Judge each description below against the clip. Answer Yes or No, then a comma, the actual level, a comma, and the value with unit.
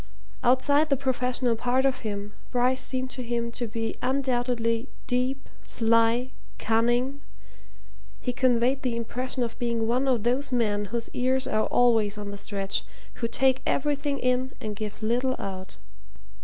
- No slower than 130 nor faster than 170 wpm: Yes, average, 150 wpm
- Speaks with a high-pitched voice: Yes, high, 245 Hz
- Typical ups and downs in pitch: No, narrow, 2.2 semitones